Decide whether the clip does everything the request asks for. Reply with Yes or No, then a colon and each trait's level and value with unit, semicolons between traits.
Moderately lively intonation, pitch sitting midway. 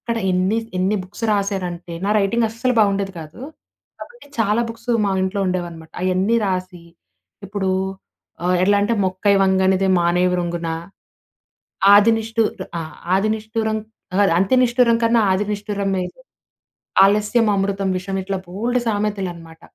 No: average, 3.1 semitones; high, 200 Hz